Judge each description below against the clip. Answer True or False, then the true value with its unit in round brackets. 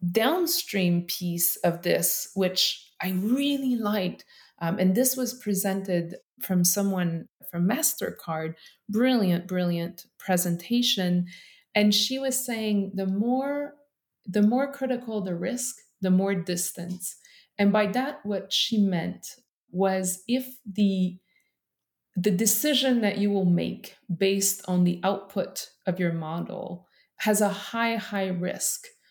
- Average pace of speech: False (125 wpm)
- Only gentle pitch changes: False (4.7 semitones)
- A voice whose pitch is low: False (195 Hz)